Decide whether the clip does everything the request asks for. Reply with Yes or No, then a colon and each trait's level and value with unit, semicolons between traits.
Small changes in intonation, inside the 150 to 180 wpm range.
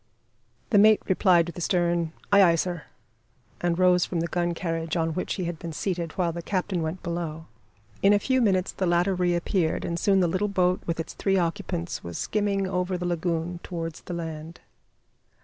No: narrow, 1.9 semitones; average, 195 wpm